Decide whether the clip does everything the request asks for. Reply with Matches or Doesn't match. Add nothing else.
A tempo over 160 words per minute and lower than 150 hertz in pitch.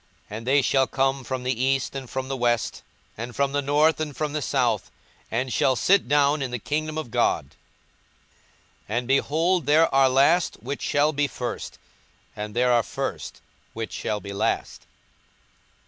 Matches